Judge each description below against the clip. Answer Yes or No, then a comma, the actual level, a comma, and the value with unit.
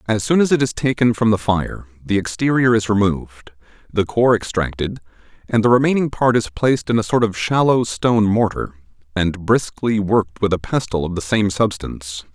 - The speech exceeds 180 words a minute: Yes, average, 190 wpm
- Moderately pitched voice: No, low, 110 Hz